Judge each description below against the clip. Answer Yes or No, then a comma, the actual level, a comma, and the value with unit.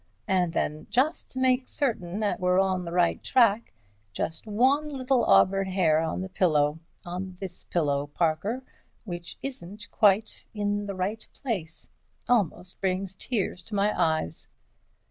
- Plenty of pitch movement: No, average, 4.2 semitones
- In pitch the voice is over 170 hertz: Yes, high, 190 Hz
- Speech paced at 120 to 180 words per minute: Yes, average, 150 wpm